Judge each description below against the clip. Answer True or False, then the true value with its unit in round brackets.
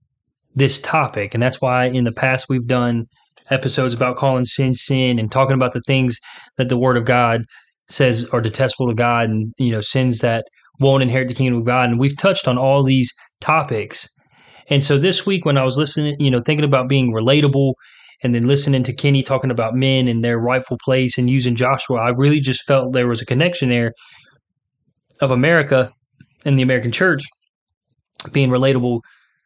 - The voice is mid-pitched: False (130 Hz)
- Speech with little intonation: True (1.8 semitones)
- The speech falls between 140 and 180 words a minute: False (190 wpm)